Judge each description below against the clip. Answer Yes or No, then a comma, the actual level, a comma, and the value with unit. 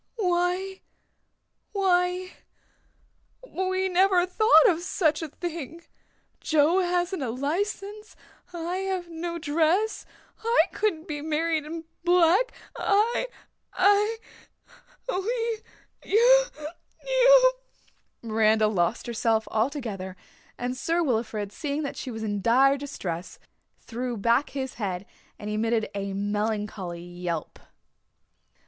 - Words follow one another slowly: Yes, slow, 110 wpm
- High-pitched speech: Yes, very high, 320 Hz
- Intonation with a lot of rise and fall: Yes, wide, 8.8 semitones